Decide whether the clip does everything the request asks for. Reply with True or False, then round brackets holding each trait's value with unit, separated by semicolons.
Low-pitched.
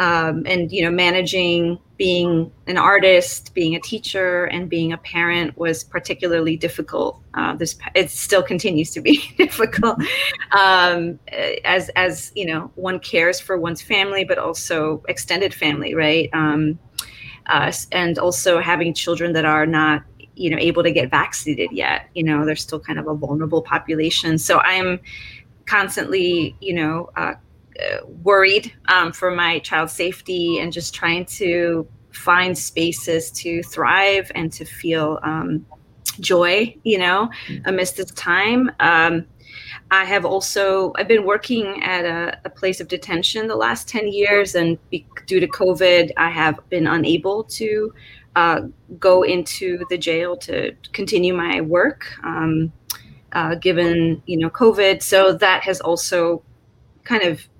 False (175 Hz)